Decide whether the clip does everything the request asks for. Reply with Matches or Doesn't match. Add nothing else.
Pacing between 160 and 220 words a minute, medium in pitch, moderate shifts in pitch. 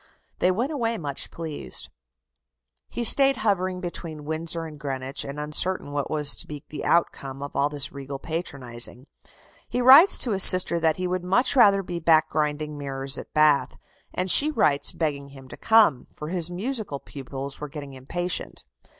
Matches